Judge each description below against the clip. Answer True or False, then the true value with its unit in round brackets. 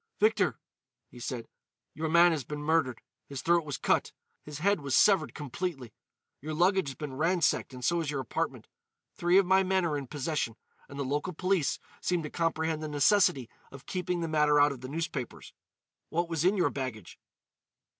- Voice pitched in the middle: True (155 Hz)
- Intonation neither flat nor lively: True (3.9 semitones)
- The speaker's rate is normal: True (185 wpm)